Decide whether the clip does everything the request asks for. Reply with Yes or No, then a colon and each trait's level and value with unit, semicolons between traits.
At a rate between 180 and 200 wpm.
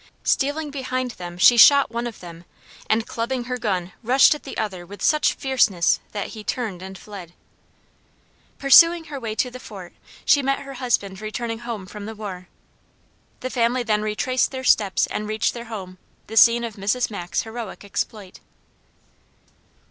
No: average, 170 wpm